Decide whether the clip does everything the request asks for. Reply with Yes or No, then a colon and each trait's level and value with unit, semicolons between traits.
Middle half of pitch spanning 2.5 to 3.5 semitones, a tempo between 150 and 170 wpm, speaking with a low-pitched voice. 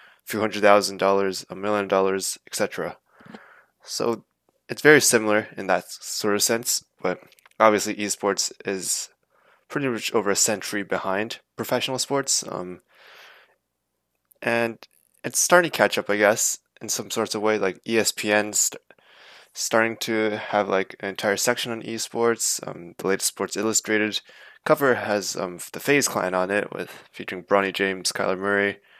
Yes: average, 2.9 semitones; average, 155 wpm; low, 105 Hz